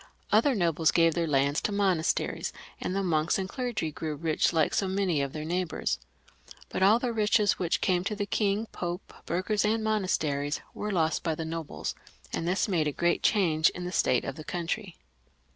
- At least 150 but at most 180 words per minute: No, average, 195 wpm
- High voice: No, medium, 175 Hz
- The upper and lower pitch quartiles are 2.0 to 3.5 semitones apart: No, average, 4.2 semitones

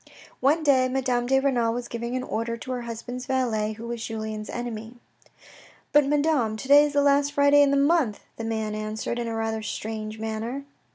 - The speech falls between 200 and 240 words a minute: Yes, fast, 205 wpm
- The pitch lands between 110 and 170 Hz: No, high, 240 Hz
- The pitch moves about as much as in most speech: Yes, average, 3.9 semitones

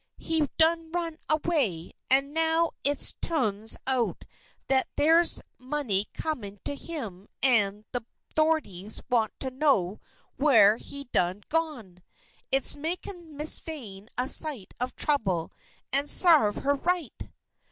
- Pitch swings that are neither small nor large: No, wide, 6.9 semitones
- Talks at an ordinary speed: No, slow, 125 wpm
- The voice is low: No, very high, 275 Hz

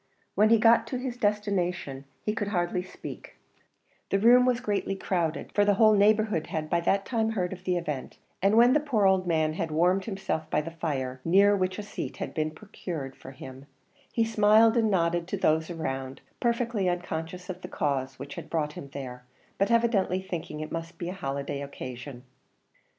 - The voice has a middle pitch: Yes, medium, 180 Hz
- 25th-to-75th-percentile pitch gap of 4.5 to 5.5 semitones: Yes, average, 5.2 semitones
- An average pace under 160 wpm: No, average, 190 wpm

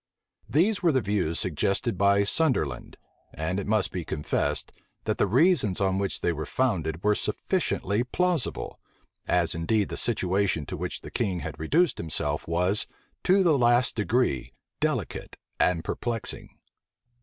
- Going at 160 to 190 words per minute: No, average, 145 wpm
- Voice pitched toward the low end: Yes, low, 100 Hz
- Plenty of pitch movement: Yes, wide, 6.3 semitones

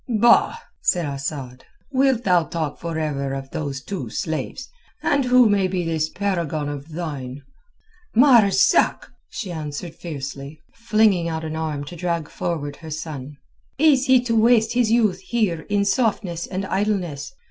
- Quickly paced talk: No, average, 145 wpm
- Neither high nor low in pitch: Yes, medium, 170 Hz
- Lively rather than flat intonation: Yes, wide, 6.3 semitones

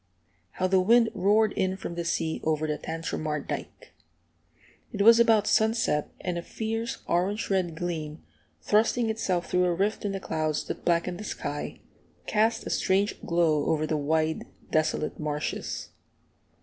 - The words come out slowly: No, average, 155 wpm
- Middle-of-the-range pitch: Yes, medium, 180 Hz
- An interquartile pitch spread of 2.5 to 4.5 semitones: No, average, 5.0 semitones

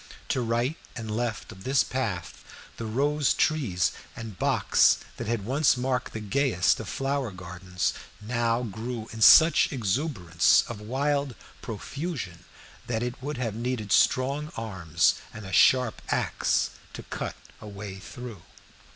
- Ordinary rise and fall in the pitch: Yes, average, 4.3 semitones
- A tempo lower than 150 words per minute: Yes, average, 140 wpm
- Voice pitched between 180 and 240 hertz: No, low, 115 Hz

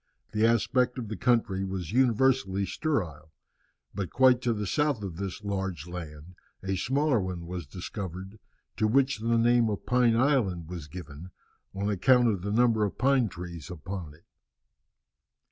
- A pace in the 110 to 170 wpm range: Yes, average, 160 wpm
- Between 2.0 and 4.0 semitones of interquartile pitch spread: No, average, 5.2 semitones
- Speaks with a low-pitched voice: Yes, low, 100 Hz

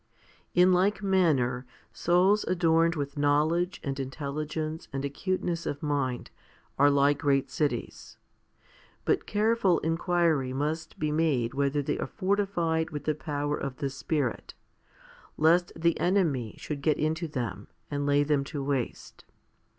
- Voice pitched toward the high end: No, medium, 150 Hz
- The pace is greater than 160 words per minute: No, slow, 135 wpm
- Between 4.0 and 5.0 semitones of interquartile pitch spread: No, average, 3.4 semitones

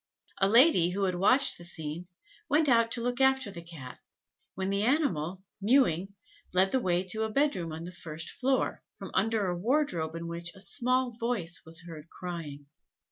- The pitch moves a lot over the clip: Yes, wide, 6.3 semitones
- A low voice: No, high, 190 Hz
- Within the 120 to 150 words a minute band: No, average, 190 wpm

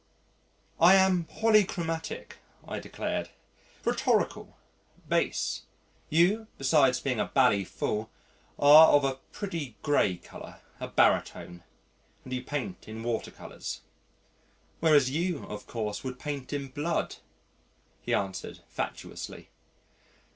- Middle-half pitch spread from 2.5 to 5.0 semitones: No, wide, 5.5 semitones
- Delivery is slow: Yes, slow, 110 wpm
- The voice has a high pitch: No, medium, 140 Hz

